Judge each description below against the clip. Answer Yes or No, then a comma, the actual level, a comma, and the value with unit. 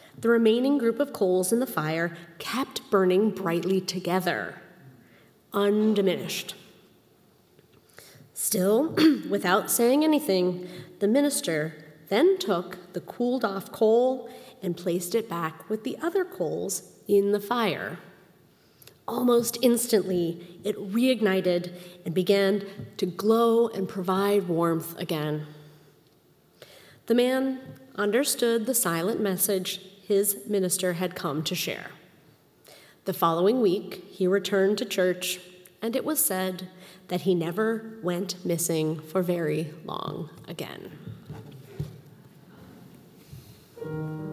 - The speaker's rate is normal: No, slow, 110 wpm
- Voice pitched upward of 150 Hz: Yes, high, 190 Hz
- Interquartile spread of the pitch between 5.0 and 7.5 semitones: No, average, 4.4 semitones